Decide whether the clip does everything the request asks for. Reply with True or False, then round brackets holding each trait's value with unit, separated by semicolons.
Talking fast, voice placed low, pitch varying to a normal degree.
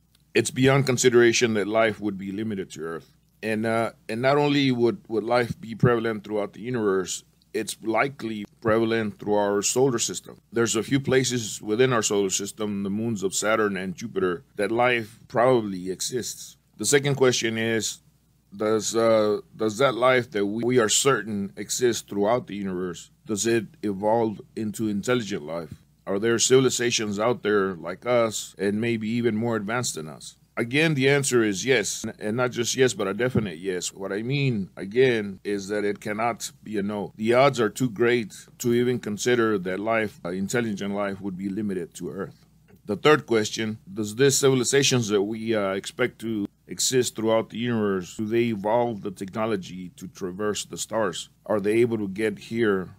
False (180 wpm; 110 Hz; 3.0 semitones)